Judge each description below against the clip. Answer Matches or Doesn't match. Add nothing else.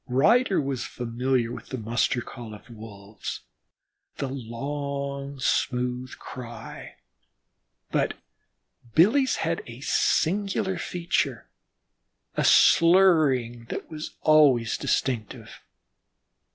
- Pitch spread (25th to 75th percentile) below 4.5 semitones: Doesn't match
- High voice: Doesn't match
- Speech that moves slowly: Matches